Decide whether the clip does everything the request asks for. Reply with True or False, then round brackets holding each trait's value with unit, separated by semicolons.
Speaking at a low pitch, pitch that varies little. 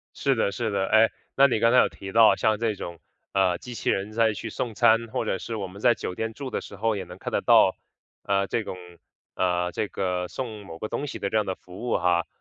False (105 Hz; 3.3 semitones)